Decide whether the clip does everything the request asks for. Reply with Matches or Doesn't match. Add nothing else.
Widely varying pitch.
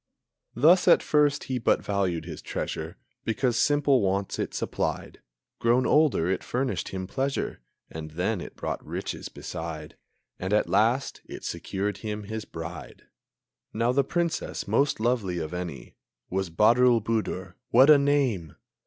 Matches